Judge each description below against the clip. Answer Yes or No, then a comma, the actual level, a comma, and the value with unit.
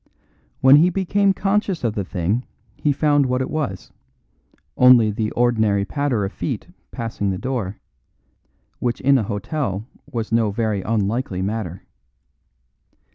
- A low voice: Yes, low, 115 Hz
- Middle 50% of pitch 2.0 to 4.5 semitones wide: No, average, 5.3 semitones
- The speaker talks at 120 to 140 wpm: Yes, slow, 135 wpm